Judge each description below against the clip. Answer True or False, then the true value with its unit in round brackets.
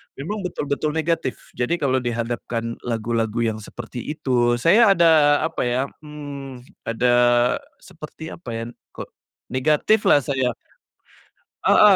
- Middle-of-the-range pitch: False (130 Hz)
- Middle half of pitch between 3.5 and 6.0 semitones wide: True (4.5 semitones)